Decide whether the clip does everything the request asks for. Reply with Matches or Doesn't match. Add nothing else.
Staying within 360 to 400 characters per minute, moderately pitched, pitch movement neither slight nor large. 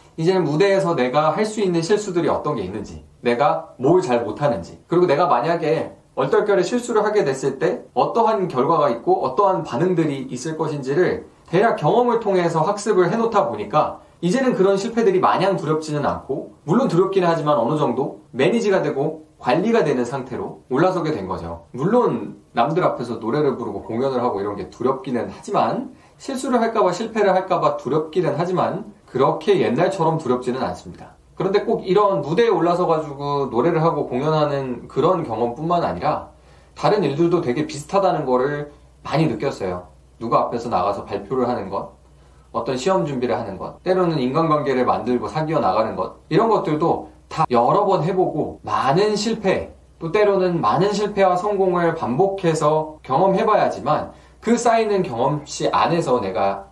Doesn't match